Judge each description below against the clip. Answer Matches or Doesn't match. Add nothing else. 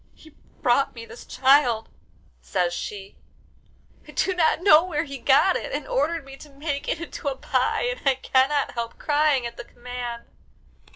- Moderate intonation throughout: Matches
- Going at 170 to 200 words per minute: Matches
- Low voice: Doesn't match